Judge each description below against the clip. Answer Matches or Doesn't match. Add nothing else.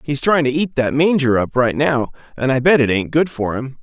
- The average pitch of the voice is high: Doesn't match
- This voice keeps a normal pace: Doesn't match